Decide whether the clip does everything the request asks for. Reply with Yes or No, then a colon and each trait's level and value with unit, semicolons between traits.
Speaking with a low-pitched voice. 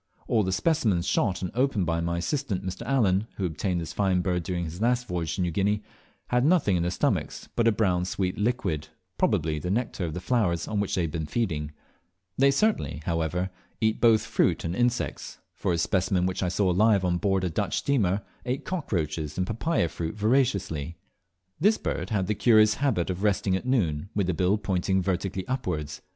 Yes: very low, 95 Hz